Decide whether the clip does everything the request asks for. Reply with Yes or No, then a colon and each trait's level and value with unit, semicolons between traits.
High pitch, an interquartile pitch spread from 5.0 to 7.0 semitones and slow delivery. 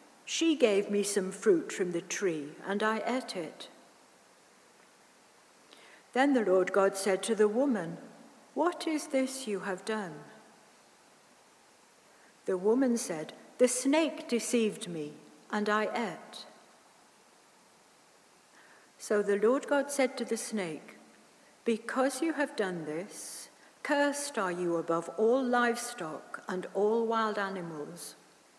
Yes: high, 220 Hz; average, 5.3 semitones; slow, 125 wpm